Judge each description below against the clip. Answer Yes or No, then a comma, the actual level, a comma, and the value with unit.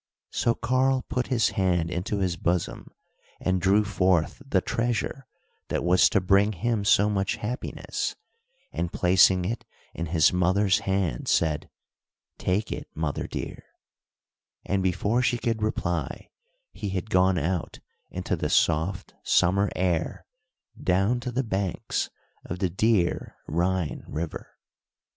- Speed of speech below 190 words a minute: Yes, slow, 135 wpm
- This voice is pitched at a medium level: No, very low, 95 Hz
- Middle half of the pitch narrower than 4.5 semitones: Yes, average, 3.3 semitones